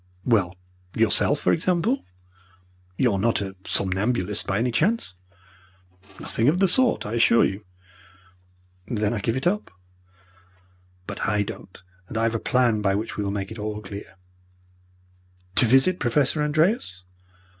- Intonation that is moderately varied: No, wide, 6.3 semitones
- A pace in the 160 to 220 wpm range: No, average, 150 wpm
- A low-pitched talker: Yes, low, 115 Hz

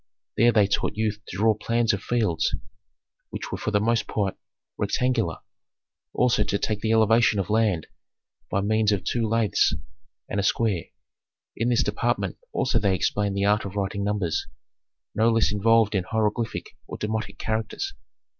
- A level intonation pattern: Yes, narrow, 2.1 semitones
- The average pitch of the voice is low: Yes, low, 105 Hz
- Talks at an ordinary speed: Yes, average, 165 wpm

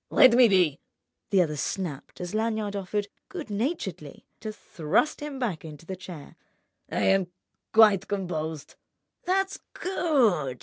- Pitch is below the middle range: No, high, 195 Hz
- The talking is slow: Yes, slow, 130 wpm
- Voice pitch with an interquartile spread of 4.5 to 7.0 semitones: Yes, wide, 5.6 semitones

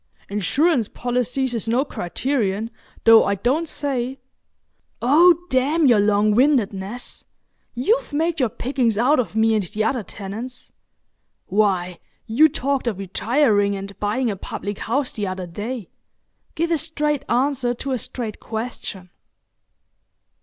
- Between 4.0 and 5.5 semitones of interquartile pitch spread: Yes, average, 4.9 semitones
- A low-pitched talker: No, high, 240 Hz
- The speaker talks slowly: Yes, slow, 130 wpm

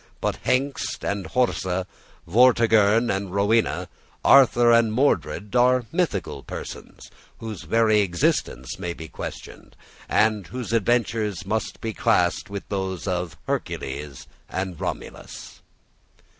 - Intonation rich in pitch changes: No, average, 4.1 semitones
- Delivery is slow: Yes, slow, 115 wpm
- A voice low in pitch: Yes, low, 105 Hz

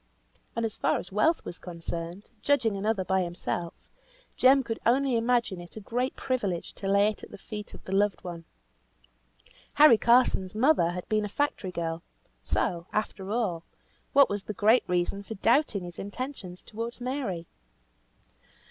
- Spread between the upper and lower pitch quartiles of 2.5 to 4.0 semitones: No, average, 4.8 semitones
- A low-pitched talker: No, high, 210 Hz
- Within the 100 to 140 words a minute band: No, average, 165 wpm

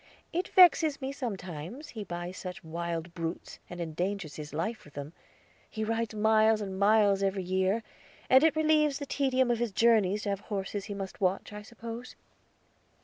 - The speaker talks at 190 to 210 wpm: No, average, 175 wpm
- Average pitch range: Yes, average, 4.5 semitones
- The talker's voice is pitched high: Yes, high, 205 Hz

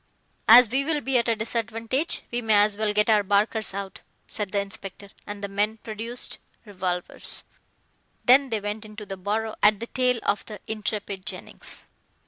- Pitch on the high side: Yes, high, 215 Hz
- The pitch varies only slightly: Yes, narrow, 2.1 semitones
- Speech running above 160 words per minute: Yes, average, 175 wpm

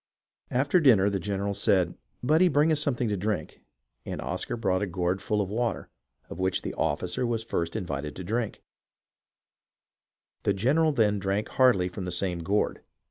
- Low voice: Yes, low, 100 Hz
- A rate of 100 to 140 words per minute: No, average, 175 wpm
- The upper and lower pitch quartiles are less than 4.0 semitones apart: No, average, 4.7 semitones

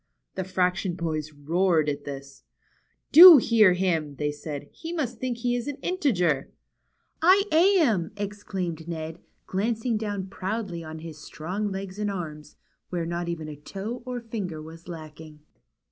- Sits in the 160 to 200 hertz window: Yes, medium, 185 Hz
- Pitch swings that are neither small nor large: No, wide, 5.9 semitones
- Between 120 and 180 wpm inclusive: Yes, average, 160 wpm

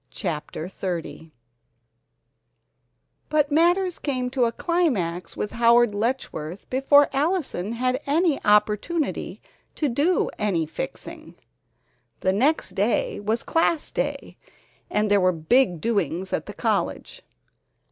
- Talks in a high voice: Yes, high, 235 Hz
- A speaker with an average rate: No, slow, 115 wpm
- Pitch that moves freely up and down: Yes, wide, 7.3 semitones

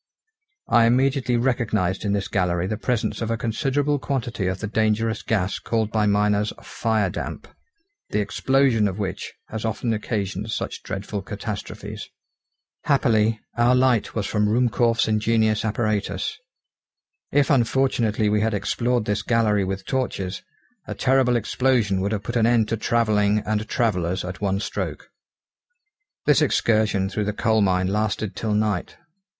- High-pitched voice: No, low, 110 Hz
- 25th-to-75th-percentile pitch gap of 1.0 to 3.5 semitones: Yes, narrow, 2.5 semitones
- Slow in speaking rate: No, average, 145 wpm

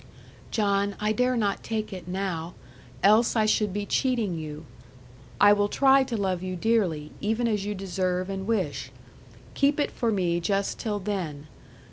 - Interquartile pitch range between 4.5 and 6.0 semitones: No, average, 3.2 semitones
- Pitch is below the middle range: No, high, 200 Hz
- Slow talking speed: No, average, 165 wpm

